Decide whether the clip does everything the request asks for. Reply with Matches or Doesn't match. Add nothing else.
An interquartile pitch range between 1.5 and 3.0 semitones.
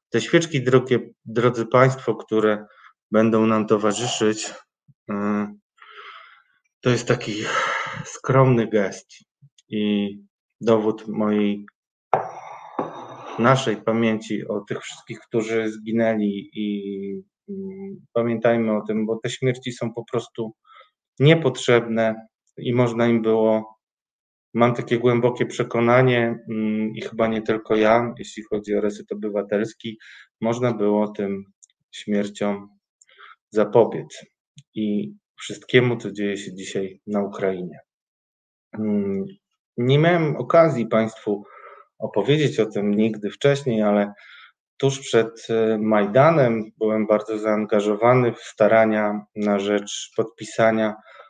Matches